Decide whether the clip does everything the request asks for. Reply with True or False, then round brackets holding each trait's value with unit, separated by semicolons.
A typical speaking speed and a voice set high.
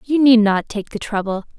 False (225 wpm; 220 Hz)